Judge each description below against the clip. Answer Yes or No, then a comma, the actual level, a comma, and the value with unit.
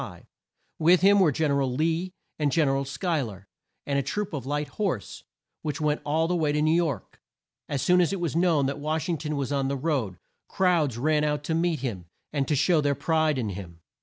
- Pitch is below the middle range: No, medium, 150 Hz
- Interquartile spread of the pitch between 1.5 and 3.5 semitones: Yes, average, 3.1 semitones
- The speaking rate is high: Yes, fast, 230 wpm